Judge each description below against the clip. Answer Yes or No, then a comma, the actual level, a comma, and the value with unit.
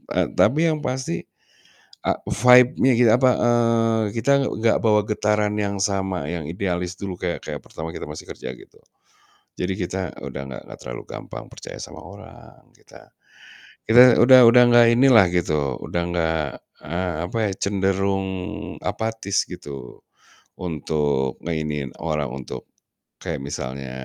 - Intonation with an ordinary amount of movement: No, wide, 6.6 semitones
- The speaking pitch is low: Yes, very low, 95 Hz